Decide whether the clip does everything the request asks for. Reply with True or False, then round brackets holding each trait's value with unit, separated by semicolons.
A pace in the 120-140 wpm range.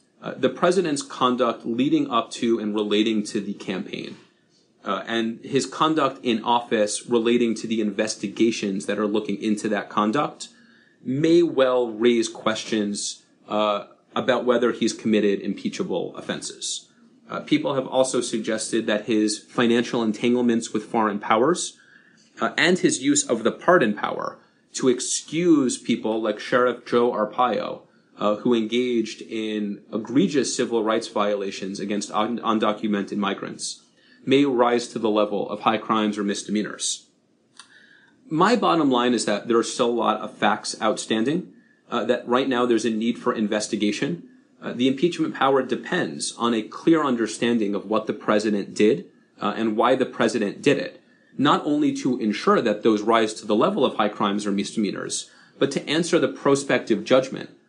False (160 wpm)